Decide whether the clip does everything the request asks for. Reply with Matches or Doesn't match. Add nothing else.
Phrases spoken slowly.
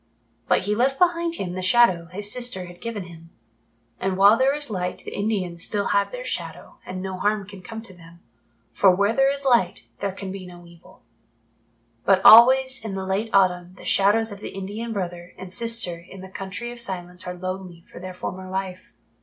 Doesn't match